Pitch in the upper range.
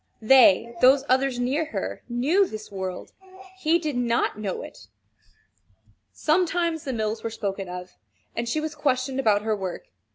Yes: high, 245 Hz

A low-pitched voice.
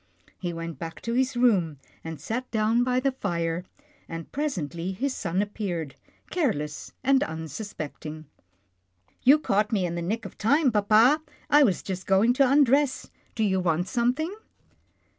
No: high, 210 Hz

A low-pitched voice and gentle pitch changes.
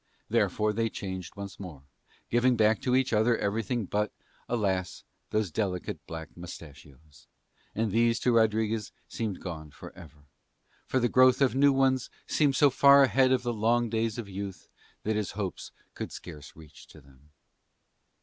No: low, 110 Hz; average, 4.7 semitones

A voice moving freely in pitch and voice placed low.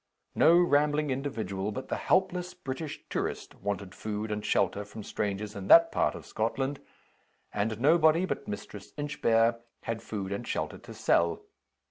Yes: wide, 6.5 semitones; low, 115 Hz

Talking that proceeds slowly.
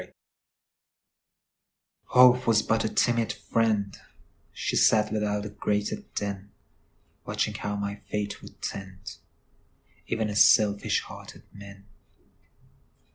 Yes: slow, 90 wpm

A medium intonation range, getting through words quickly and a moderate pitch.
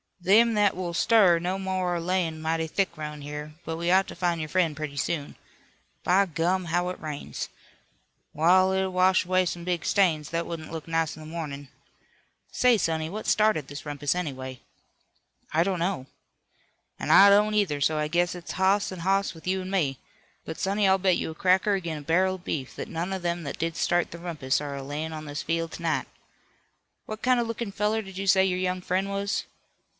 Yes: average, 3.2 semitones; fast, 210 wpm; medium, 175 Hz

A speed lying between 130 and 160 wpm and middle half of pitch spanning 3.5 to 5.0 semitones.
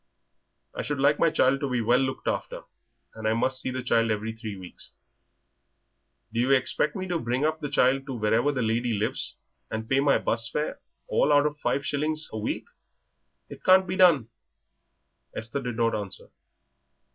No: average, 185 wpm; average, 4.3 semitones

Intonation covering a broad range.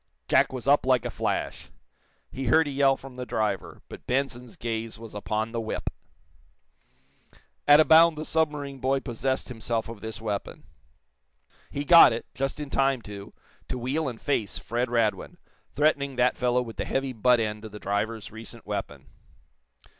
No: average, 3.4 semitones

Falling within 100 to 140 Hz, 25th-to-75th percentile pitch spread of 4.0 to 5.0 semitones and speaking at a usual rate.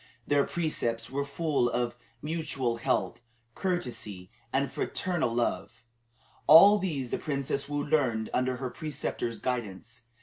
No: low, 135 Hz; average, 4.6 semitones; slow, 125 wpm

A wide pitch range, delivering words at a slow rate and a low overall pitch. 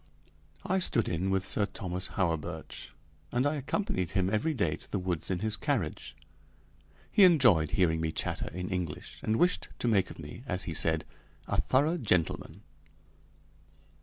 No: wide, 6.1 semitones; average, 165 wpm; very low, 95 Hz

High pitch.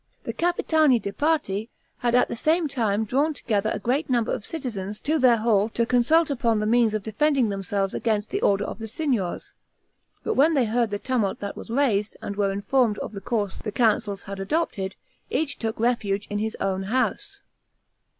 Yes: high, 225 Hz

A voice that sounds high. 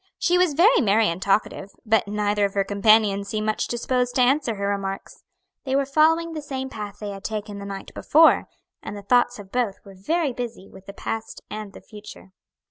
Yes: high, 215 Hz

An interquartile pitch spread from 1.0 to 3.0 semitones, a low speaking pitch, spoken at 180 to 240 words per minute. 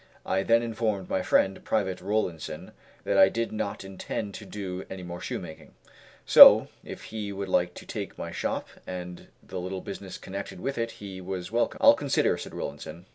Yes: narrow, 2.4 semitones; very low, 95 Hz; average, 185 wpm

